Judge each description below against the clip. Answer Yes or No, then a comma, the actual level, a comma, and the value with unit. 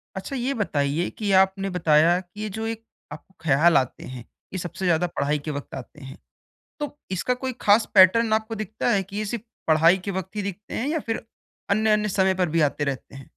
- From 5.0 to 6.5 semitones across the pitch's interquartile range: Yes, average, 5.3 semitones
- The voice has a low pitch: No, high, 190 Hz